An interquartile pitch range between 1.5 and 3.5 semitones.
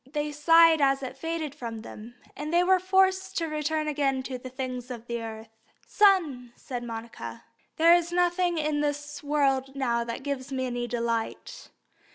No: average, 4.8 semitones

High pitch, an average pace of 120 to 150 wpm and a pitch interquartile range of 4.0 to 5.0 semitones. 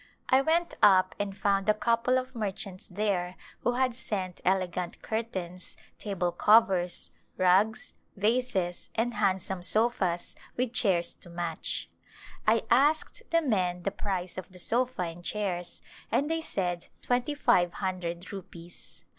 Yes: high, 195 Hz; average, 145 wpm; average, 4.6 semitones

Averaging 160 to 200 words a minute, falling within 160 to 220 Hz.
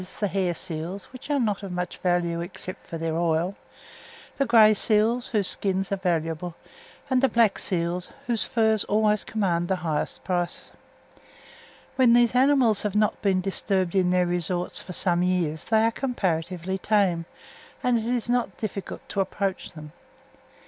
Yes: average, 165 wpm; high, 190 Hz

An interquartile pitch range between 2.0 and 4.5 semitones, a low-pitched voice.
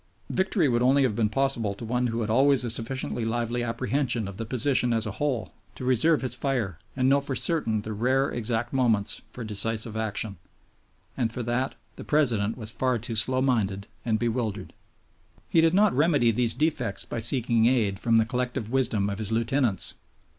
Yes: average, 3.0 semitones; low, 120 Hz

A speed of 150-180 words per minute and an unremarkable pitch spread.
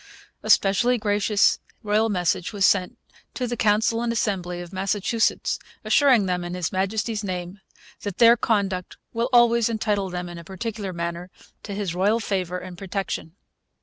Yes: average, 160 wpm; average, 3.4 semitones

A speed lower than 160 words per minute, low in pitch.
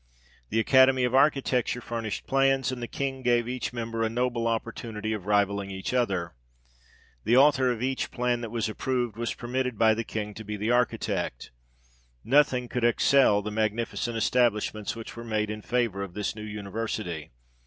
No: average, 175 wpm; low, 115 Hz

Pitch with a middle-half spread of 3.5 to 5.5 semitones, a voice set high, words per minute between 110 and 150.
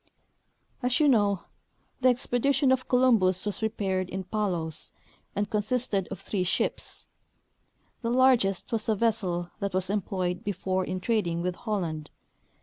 Yes: average, 4.1 semitones; high, 205 Hz; average, 140 wpm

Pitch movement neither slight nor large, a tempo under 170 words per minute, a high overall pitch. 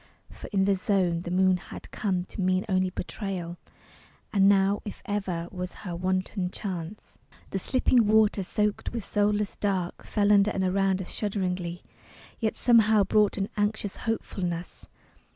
No: narrow, 2.2 semitones; average, 150 wpm; high, 195 Hz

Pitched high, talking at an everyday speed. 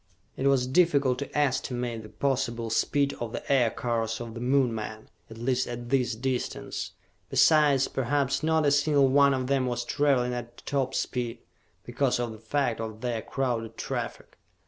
No: low, 125 Hz; average, 170 wpm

